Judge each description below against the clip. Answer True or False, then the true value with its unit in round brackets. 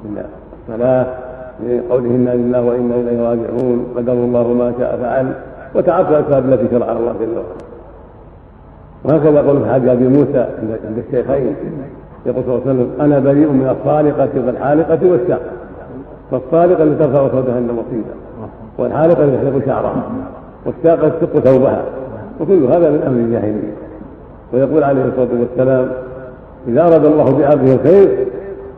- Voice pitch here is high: False (130 Hz)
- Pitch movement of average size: True (3.4 semitones)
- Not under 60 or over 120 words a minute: False (130 wpm)